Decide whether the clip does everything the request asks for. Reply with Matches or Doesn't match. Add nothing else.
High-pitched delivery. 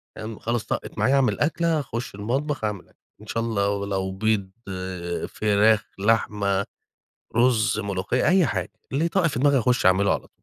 Doesn't match